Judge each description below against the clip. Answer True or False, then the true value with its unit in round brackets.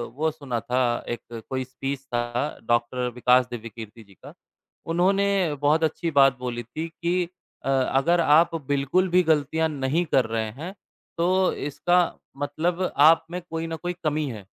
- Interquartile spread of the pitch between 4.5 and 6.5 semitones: True (4.8 semitones)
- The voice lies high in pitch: False (145 Hz)